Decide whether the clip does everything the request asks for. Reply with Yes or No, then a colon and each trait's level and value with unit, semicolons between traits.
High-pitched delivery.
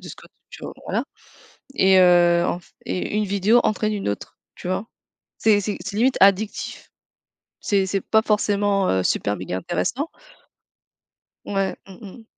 Yes: high, 195 Hz